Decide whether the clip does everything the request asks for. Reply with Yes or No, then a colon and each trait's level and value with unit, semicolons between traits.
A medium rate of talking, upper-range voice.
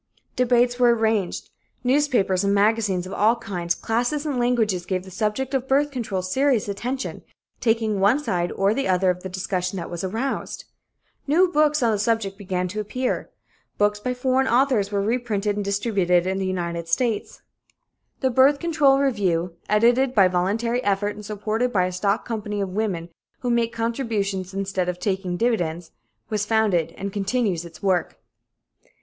Yes: average, 165 wpm; high, 210 Hz